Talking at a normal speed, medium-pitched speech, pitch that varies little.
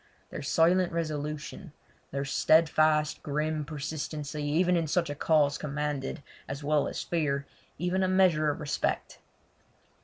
No: slow, 130 wpm; medium, 150 Hz; narrow, 2.2 semitones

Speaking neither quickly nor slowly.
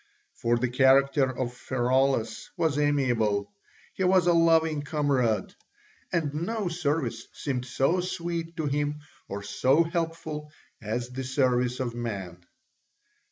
No: slow, 125 wpm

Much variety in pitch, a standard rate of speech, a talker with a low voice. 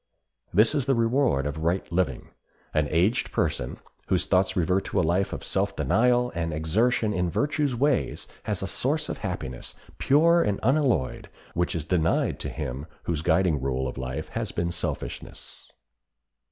Yes: wide, 7.6 semitones; average, 165 wpm; very low, 90 Hz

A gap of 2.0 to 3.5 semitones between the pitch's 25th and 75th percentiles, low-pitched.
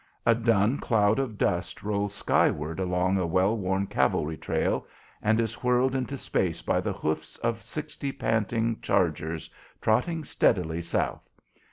No: average, 4.2 semitones; low, 105 Hz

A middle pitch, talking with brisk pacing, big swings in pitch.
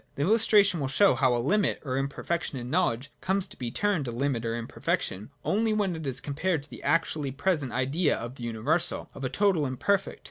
Yes: medium, 145 Hz; fast, 225 wpm; wide, 6.6 semitones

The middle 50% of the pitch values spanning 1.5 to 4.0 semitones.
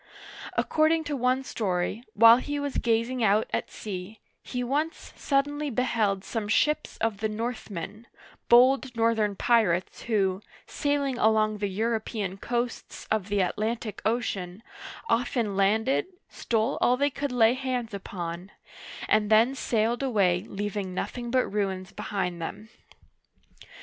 Yes: average, 3.7 semitones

